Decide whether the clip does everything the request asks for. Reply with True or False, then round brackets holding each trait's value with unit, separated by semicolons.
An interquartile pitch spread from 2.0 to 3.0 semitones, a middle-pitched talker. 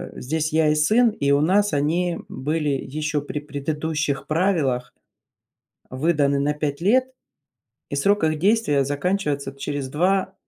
False (3.9 semitones; 150 Hz)